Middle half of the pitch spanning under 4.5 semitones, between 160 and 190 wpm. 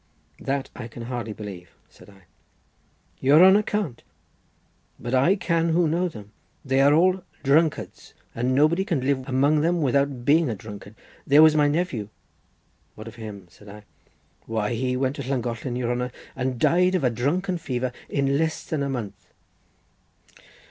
No: average, 4.9 semitones; average, 165 wpm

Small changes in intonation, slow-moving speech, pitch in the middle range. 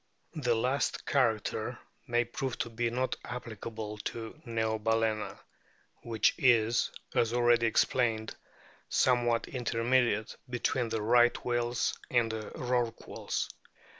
No: narrow, 1.5 semitones; slow, 110 wpm; low, 115 Hz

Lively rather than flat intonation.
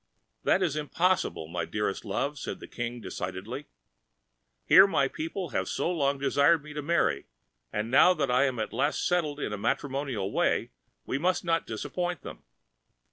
Yes: wide, 6.9 semitones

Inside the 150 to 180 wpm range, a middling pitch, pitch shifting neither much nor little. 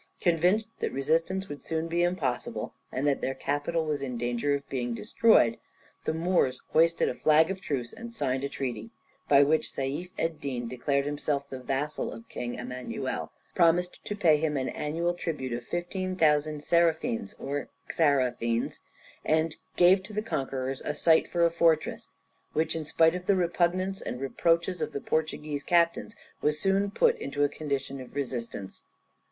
Yes: average, 170 wpm; medium, 150 Hz; average, 4.2 semitones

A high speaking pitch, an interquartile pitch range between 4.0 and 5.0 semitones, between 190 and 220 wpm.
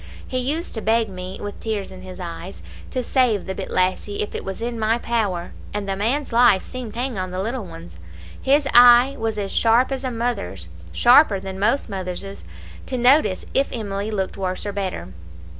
Yes: high, 210 Hz; average, 4.3 semitones; average, 200 wpm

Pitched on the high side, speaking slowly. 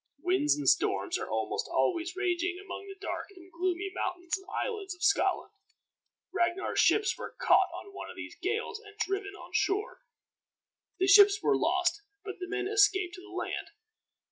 No: very high, 380 Hz; average, 170 wpm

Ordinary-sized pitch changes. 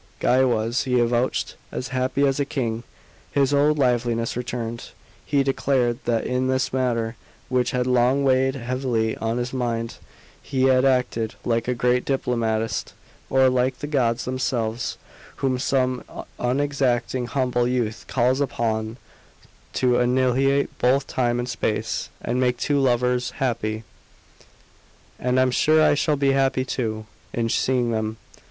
No: narrow, 1.9 semitones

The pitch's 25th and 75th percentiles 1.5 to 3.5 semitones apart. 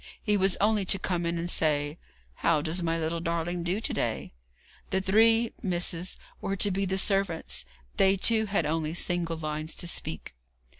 Yes: average, 3.0 semitones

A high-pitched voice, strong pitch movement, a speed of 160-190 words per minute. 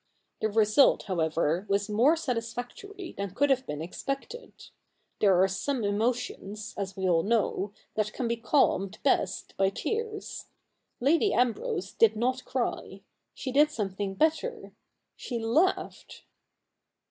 No: high, 225 Hz; wide, 5.8 semitones; slow, 135 wpm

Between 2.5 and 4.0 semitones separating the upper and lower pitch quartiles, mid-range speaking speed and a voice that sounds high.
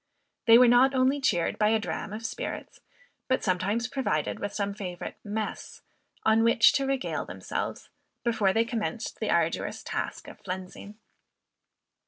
Yes: average, 3.5 semitones; average, 150 wpm; high, 225 Hz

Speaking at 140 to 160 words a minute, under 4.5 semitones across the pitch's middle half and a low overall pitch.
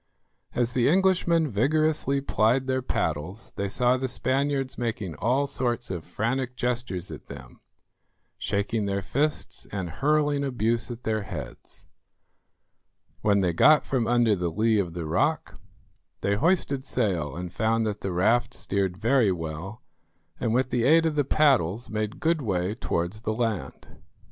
No: average, 155 wpm; average, 5.2 semitones; low, 115 Hz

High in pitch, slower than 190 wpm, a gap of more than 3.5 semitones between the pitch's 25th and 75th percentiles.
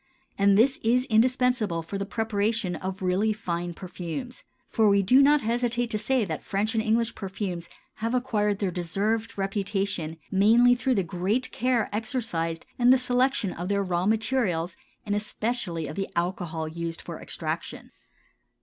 Yes: high, 205 Hz; average, 160 wpm; average, 4.5 semitones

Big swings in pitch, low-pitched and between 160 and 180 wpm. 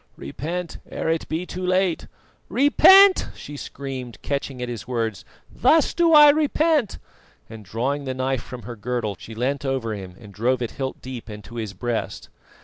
Yes: wide, 7.2 semitones; low, 130 Hz; average, 170 wpm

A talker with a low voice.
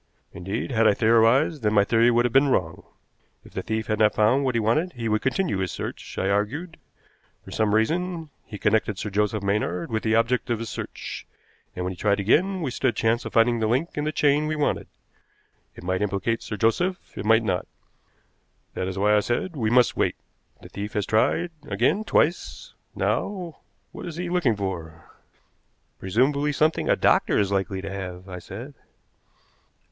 Yes: low, 115 Hz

